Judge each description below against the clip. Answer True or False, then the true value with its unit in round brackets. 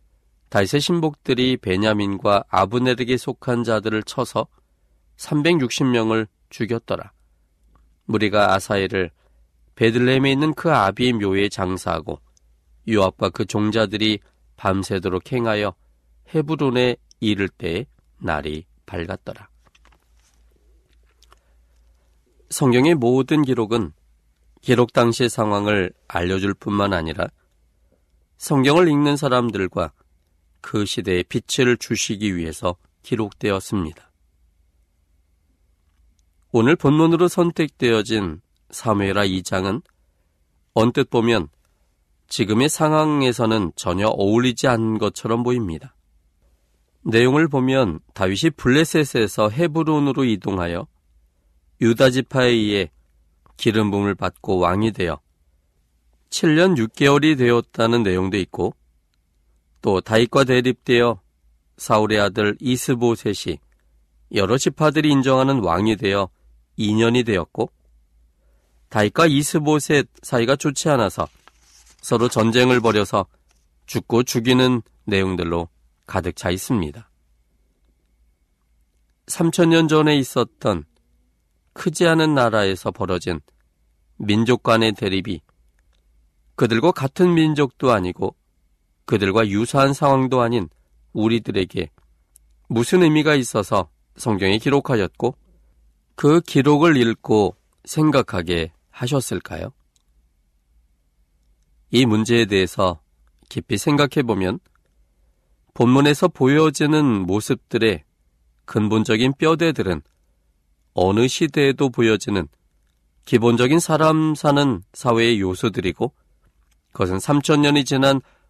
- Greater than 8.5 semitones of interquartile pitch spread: True (9.0 semitones)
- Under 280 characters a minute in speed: True (230 characters per minute)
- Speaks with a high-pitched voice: False (100 Hz)